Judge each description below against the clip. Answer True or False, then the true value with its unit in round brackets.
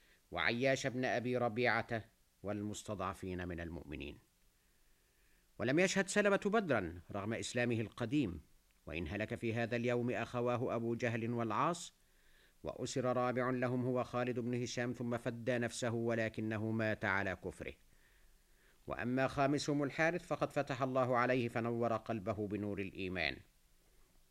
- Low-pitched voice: True (120 Hz)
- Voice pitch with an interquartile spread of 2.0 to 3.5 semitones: True (3.2 semitones)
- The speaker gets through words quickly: False (120 wpm)